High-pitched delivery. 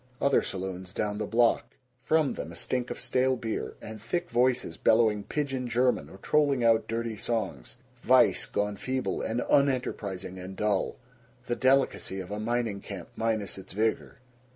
No: low, 115 Hz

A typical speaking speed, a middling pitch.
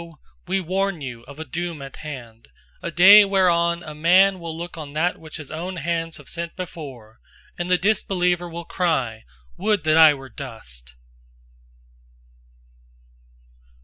Yes: average, 145 wpm; medium, 165 Hz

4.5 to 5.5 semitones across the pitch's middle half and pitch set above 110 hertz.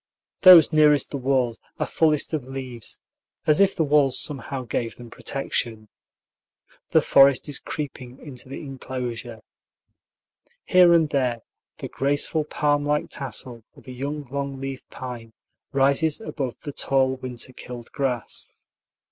No: average, 2.8 semitones; low, 135 Hz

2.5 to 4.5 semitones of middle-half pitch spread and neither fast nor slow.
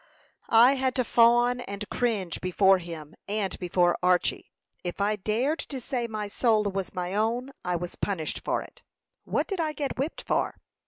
No: average, 5.1 semitones; average, 175 wpm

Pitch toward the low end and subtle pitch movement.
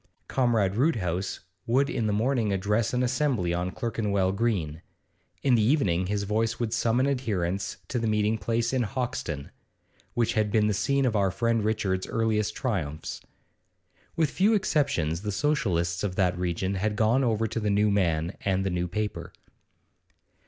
No: low, 105 Hz; average, 4.0 semitones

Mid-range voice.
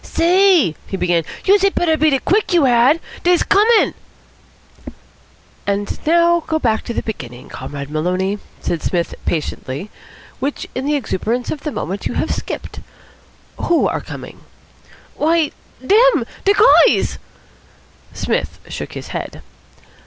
No: very high, 280 Hz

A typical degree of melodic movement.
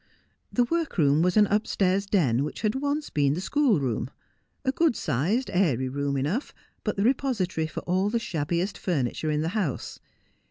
No: wide, 7.4 semitones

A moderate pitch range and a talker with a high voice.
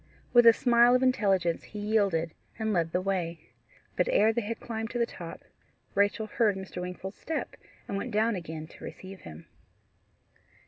Yes: average, 4.0 semitones; high, 200 Hz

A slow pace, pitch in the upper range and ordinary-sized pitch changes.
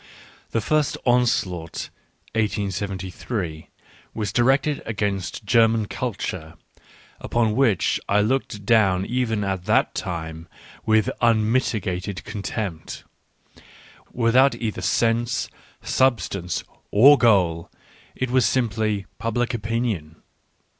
No: slow, 100 wpm; low, 110 Hz; average, 3.8 semitones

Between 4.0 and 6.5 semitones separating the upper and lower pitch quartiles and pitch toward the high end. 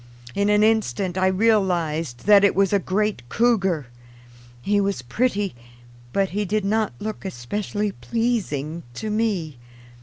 No: average, 3.2 semitones; high, 200 Hz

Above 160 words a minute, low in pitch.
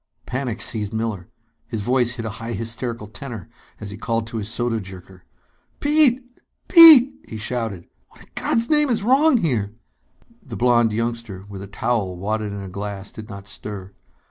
Yes: average, 170 wpm; low, 115 Hz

